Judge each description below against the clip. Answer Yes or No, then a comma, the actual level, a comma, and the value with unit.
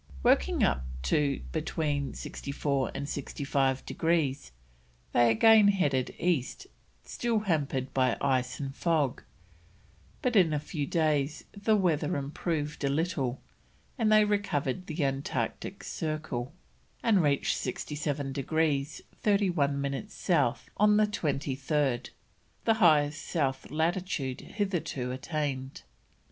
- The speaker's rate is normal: No, slow, 115 wpm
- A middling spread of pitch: Yes, average, 4.2 semitones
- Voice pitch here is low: No, medium, 150 Hz